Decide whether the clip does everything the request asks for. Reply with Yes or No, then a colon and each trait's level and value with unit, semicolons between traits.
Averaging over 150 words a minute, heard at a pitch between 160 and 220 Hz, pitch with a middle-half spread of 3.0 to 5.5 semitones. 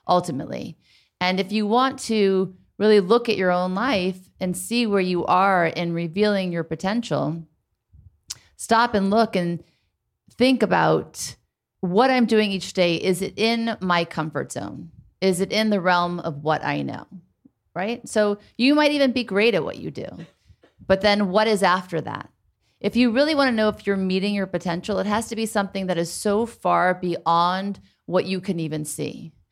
Yes: average, 185 wpm; high, 190 Hz; average, 3.9 semitones